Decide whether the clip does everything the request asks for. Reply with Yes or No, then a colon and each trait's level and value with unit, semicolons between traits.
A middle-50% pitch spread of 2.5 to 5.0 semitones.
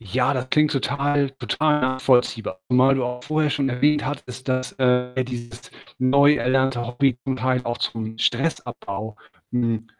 No: narrow, 2.1 semitones